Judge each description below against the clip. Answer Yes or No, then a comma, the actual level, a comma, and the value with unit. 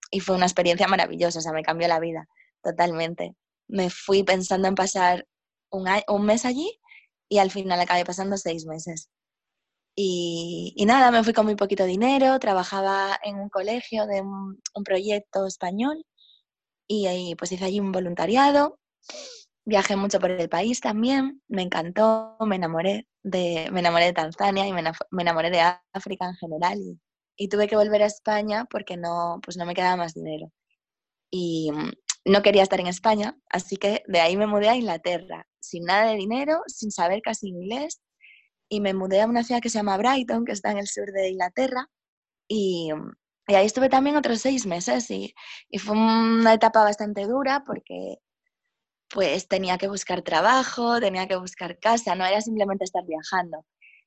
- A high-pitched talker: Yes, high, 195 Hz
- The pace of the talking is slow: No, average, 180 wpm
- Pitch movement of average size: Yes, average, 3.6 semitones